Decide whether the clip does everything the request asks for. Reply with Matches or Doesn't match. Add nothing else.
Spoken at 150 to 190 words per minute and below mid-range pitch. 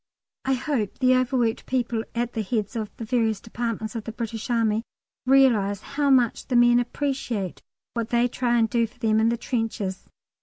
Doesn't match